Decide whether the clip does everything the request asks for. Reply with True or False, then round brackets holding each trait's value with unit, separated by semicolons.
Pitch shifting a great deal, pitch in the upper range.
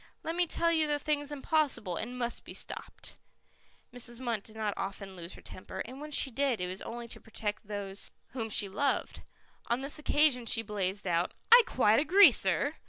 True (6.1 semitones; 235 Hz)